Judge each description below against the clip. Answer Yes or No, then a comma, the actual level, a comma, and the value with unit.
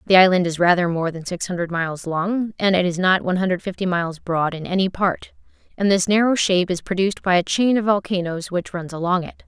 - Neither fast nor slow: No, fast, 235 wpm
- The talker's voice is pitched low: No, medium, 185 Hz